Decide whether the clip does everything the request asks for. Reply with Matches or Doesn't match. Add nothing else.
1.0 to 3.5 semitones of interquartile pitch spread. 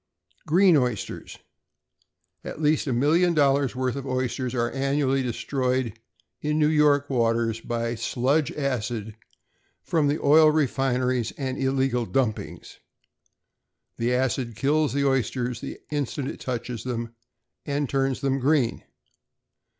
Matches